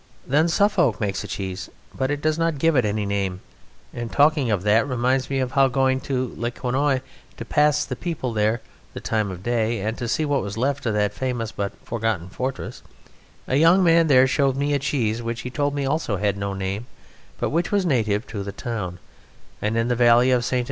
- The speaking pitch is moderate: No, low, 125 Hz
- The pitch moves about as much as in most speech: Yes, average, 4.8 semitones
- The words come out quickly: Yes, fast, 210 wpm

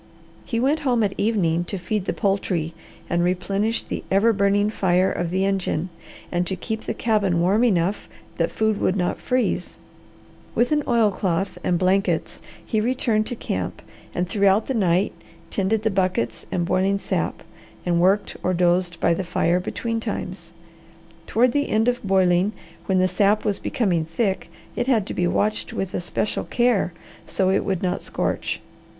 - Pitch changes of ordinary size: Yes, average, 3.4 semitones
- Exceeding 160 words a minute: Yes, average, 170 wpm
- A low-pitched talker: No, high, 195 Hz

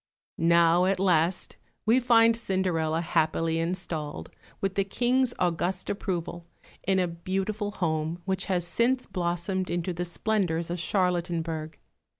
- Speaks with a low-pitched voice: No, medium, 180 Hz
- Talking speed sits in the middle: No, slow, 130 wpm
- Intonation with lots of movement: No, narrow, 2.6 semitones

